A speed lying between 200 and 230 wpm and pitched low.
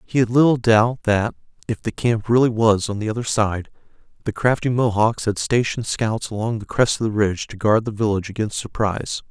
Yes: fast, 205 wpm; low, 110 Hz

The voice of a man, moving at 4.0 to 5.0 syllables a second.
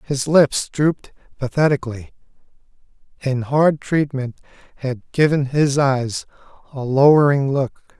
Yes: male; 4.3 syllables/s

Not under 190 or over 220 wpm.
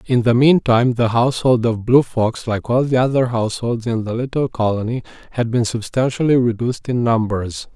No: average, 180 wpm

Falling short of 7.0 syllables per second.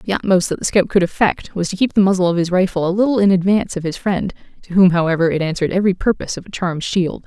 No: 7.1 syllables/s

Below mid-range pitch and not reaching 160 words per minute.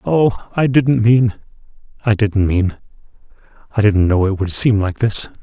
Yes: low, 110 Hz; average, 145 wpm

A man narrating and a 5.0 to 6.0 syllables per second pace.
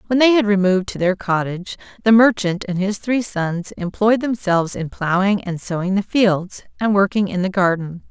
No: female; 5.1 syllables/s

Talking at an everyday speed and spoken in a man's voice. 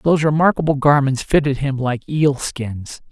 Yes: average, 155 wpm; male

